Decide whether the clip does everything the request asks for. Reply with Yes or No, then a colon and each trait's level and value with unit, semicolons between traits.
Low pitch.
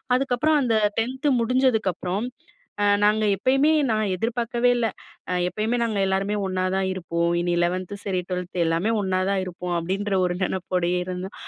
No: high, 195 Hz